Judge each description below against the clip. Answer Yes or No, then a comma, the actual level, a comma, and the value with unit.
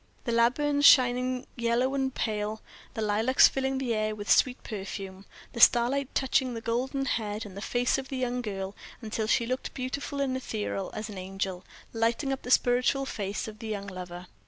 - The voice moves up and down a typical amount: Yes, average, 3.7 semitones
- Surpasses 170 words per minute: Yes, average, 180 wpm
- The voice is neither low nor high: No, high, 235 Hz